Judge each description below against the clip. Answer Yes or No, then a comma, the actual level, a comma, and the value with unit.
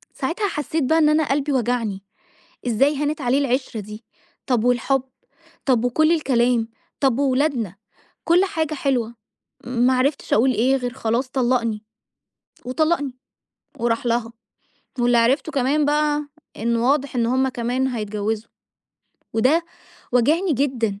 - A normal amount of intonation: Yes, average, 3.7 semitones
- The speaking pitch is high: Yes, very high, 255 Hz